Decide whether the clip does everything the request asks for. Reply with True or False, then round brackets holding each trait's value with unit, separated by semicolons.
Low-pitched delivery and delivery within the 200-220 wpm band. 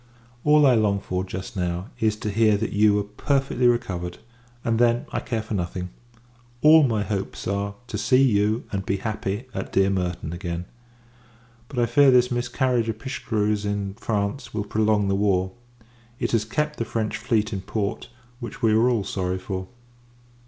False (105 Hz; 180 wpm)